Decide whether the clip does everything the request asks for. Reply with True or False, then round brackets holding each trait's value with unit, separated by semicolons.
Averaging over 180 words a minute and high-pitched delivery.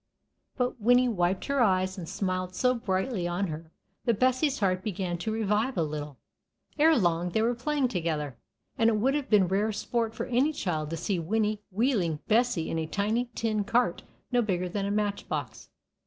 True (190 wpm; 210 Hz)